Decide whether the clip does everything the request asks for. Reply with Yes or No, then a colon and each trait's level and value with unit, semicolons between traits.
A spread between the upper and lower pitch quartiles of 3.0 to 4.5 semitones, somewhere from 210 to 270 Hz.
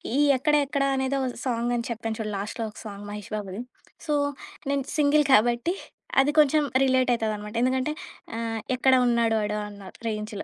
Yes: average, 3.8 semitones; high, 235 Hz